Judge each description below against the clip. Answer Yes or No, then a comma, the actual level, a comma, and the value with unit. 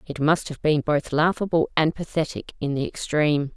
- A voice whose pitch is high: No, medium, 155 Hz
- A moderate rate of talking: Yes, average, 185 wpm